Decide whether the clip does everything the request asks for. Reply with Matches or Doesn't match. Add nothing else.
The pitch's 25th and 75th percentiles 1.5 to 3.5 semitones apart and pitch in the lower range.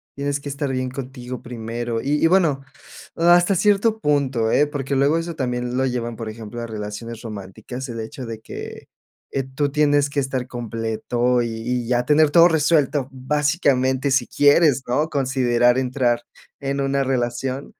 Matches